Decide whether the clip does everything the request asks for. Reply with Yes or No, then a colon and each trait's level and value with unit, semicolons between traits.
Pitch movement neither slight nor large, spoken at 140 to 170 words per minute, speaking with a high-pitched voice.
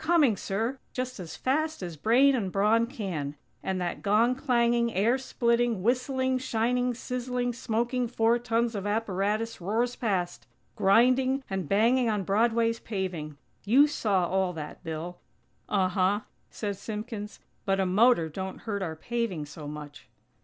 Yes: average, 4.4 semitones; average, 145 wpm; high, 225 Hz